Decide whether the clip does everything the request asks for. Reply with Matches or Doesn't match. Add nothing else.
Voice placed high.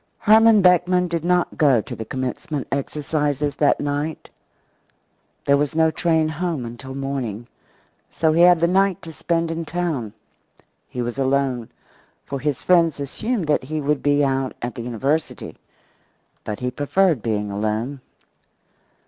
Doesn't match